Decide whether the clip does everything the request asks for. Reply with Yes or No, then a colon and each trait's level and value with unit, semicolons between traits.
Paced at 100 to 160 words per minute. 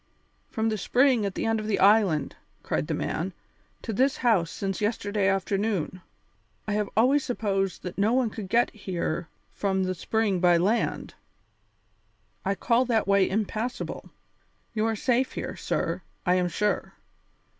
Yes: average, 155 wpm